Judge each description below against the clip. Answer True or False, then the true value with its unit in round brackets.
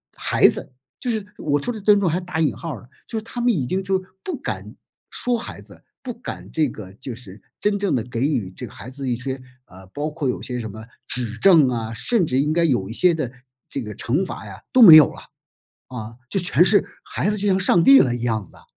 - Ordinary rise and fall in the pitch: False (8.3 semitones)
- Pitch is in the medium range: True (145 Hz)